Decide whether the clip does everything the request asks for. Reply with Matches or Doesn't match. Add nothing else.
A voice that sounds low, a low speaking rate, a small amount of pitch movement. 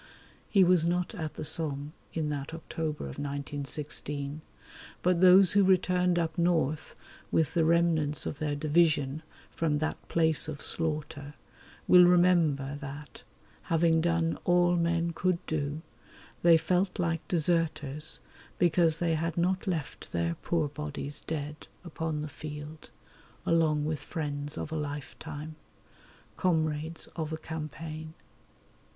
Doesn't match